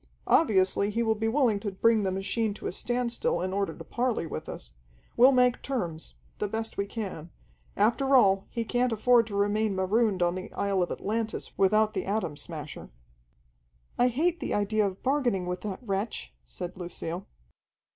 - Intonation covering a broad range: No, average, 3.8 semitones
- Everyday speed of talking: Yes, average, 175 wpm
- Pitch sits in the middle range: No, high, 210 Hz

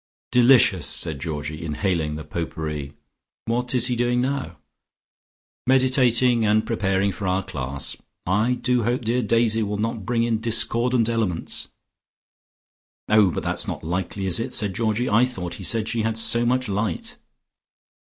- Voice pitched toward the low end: Yes, low, 110 Hz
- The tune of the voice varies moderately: Yes, average, 4.6 semitones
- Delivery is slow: No, average, 155 wpm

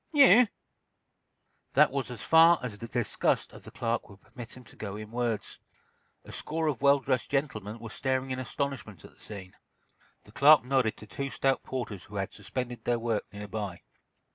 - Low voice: Yes, low, 120 Hz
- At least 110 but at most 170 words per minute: No, average, 185 wpm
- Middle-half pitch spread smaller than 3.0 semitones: No, average, 4.2 semitones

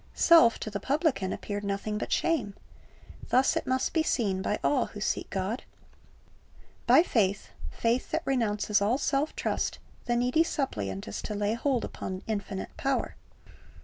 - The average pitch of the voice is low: No, high, 225 Hz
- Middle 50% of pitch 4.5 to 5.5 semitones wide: Yes, average, 5.0 semitones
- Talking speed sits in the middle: Yes, average, 165 wpm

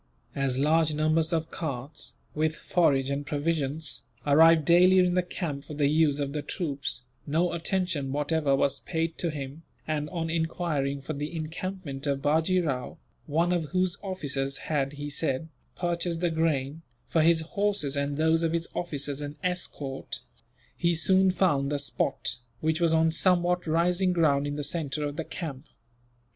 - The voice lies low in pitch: No, medium, 155 Hz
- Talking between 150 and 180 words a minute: Yes, average, 165 wpm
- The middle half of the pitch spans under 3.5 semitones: Yes, average, 3.0 semitones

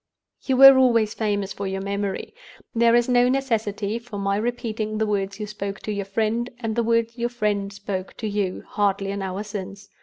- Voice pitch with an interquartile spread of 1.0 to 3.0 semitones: Yes, narrow, 2.6 semitones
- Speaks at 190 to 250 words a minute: Yes, average, 200 wpm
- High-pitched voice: Yes, high, 210 Hz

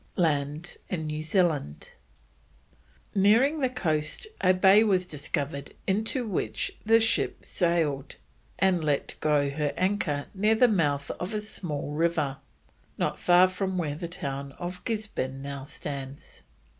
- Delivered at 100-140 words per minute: Yes, slow, 135 wpm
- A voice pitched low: No, medium, 170 Hz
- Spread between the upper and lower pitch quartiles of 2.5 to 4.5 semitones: No, average, 5.2 semitones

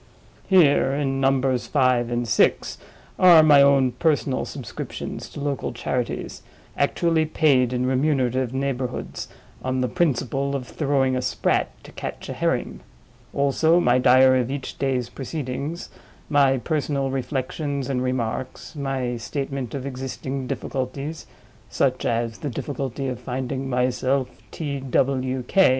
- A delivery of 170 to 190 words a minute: No, slow, 135 wpm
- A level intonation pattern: Yes, narrow, 1.8 semitones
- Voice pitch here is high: No, low, 135 Hz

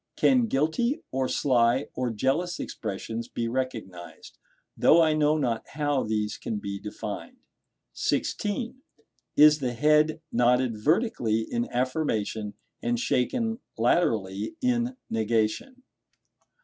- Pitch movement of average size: No, wide, 6.6 semitones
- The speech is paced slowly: Yes, slow, 110 wpm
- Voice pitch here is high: No, low, 130 Hz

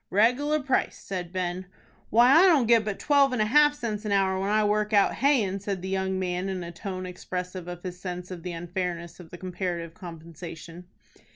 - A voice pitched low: No, high, 190 Hz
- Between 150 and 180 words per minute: No, fast, 205 wpm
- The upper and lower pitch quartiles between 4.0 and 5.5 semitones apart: No, average, 3.3 semitones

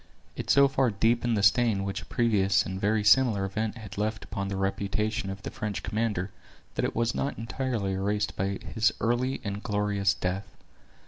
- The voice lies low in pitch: Yes, low, 105 Hz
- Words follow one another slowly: No, average, 185 wpm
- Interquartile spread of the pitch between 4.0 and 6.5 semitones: No, average, 2.8 semitones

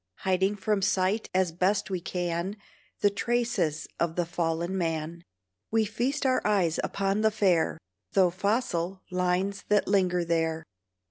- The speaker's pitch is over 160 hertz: Yes, medium, 185 Hz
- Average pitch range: Yes, average, 3.2 semitones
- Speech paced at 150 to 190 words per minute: No, average, 140 wpm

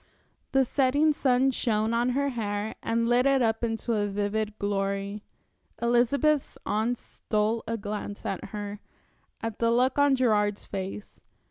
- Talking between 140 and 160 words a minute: Yes, average, 145 wpm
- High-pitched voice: Yes, high, 225 Hz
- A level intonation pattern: No, average, 3.3 semitones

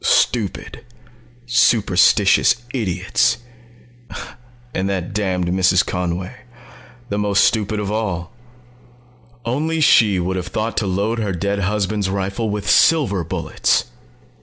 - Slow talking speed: Yes, slow, 110 wpm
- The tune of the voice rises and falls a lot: No, average, 2.8 semitones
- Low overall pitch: Yes, low, 100 Hz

